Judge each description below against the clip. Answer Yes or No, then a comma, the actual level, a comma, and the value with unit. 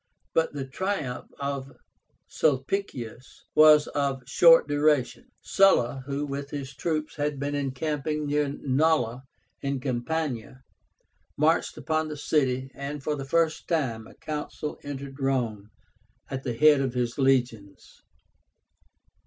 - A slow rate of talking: Yes, slow, 125 wpm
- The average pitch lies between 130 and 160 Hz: Yes, medium, 140 Hz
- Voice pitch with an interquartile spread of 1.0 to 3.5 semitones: Yes, average, 2.7 semitones